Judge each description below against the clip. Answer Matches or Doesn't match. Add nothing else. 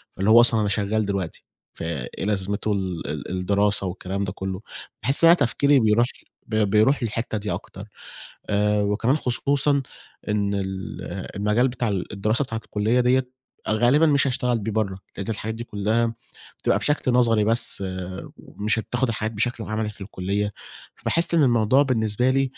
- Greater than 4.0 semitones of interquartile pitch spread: Doesn't match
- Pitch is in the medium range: Doesn't match